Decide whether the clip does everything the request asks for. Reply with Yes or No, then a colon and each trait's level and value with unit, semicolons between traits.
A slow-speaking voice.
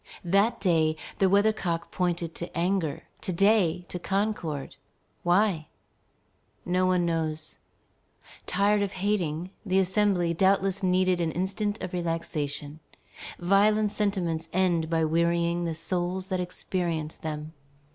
Yes: slow, 125 wpm